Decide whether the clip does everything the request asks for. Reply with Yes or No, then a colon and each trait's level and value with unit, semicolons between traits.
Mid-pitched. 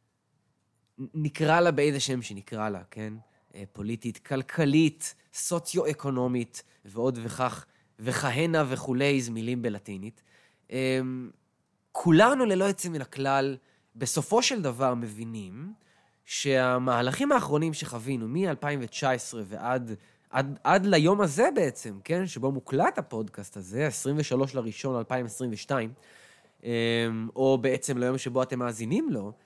No: low, 130 Hz